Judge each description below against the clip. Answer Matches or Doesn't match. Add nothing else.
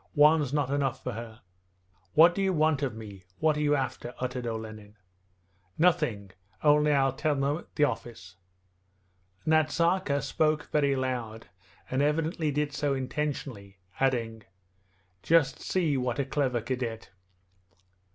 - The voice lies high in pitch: Doesn't match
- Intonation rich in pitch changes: Doesn't match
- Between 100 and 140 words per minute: Matches